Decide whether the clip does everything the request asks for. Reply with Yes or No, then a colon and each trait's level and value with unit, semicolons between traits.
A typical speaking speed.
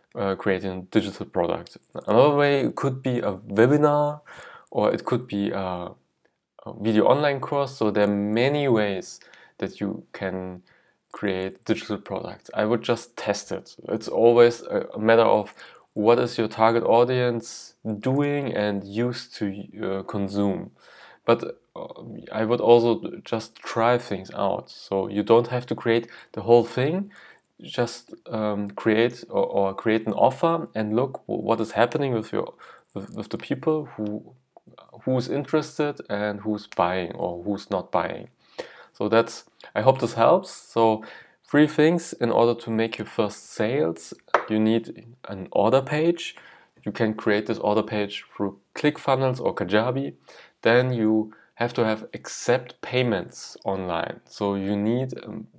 Yes: average, 155 wpm